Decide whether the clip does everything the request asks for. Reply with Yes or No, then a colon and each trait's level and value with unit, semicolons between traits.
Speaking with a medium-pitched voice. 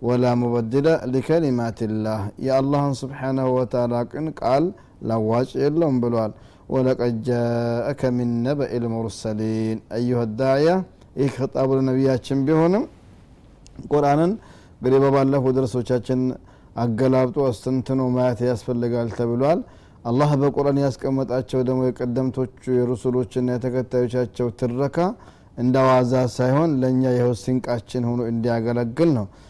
No: low, 125 Hz